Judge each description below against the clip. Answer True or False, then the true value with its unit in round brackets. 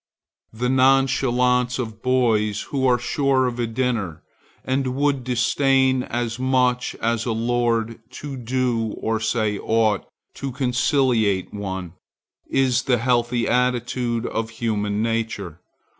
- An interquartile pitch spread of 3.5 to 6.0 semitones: False (2.4 semitones)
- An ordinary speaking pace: False (125 wpm)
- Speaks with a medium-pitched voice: False (120 Hz)